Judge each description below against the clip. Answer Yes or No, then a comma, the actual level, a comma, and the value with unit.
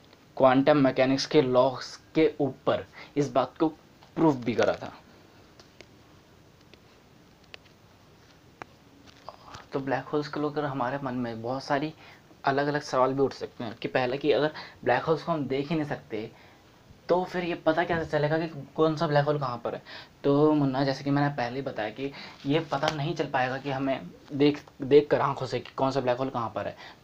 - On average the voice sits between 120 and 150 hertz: Yes, medium, 140 Hz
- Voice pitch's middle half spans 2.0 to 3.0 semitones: Yes, narrow, 2.4 semitones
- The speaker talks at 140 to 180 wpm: No, fast, 190 wpm